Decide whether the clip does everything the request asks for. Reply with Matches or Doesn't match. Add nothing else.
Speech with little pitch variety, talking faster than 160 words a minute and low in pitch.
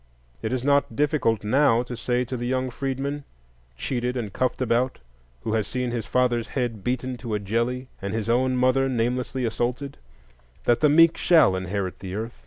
Matches